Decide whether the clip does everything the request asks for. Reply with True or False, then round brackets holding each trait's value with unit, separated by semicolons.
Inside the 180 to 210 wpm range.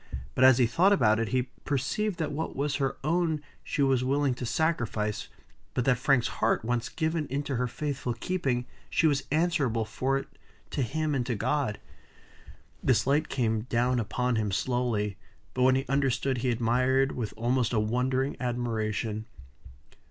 False (165 wpm)